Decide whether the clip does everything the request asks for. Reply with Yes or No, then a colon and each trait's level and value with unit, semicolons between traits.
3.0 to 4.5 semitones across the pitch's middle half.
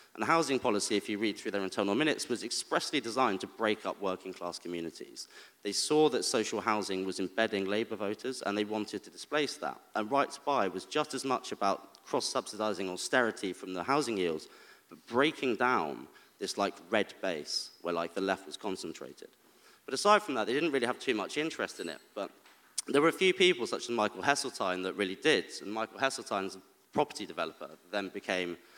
No: wide, 5.4 semitones